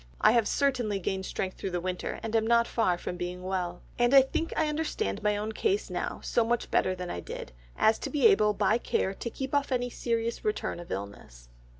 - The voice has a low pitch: No, high, 220 Hz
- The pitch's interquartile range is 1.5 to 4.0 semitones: No, average, 5.2 semitones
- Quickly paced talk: Yes, fast, 225 wpm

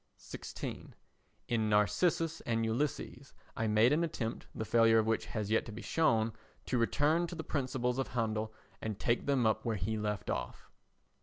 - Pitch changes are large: No, average, 3.7 semitones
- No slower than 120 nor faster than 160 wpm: No, average, 175 wpm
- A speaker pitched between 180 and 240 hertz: No, low, 115 Hz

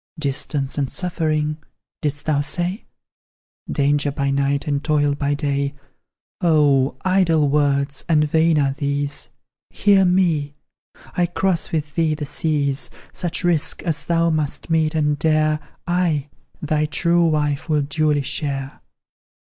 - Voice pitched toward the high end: No, medium, 150 Hz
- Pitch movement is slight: Yes, narrow, 2.3 semitones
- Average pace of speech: No, slow, 130 wpm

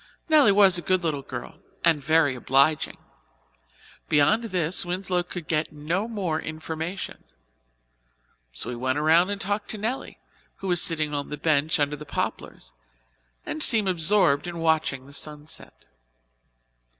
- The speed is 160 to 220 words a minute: No, average, 145 wpm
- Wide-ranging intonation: No, average, 4.2 semitones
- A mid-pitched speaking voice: Yes, medium, 160 Hz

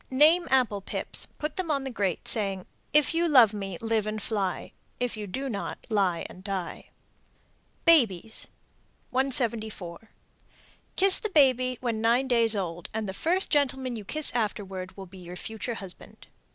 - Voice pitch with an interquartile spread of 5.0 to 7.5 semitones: Yes, average, 5.3 semitones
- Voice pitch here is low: No, high, 225 Hz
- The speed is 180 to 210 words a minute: No, average, 160 wpm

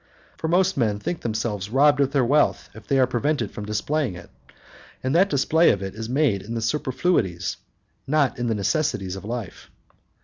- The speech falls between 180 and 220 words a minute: Yes, average, 190 wpm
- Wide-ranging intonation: Yes, wide, 6.0 semitones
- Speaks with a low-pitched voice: Yes, low, 125 Hz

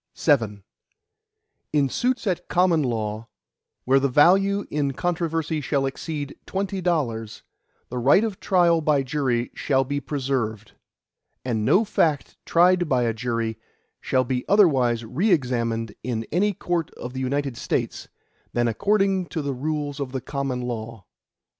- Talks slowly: No, average, 145 wpm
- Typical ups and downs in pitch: No, wide, 5.7 semitones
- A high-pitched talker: No, medium, 140 Hz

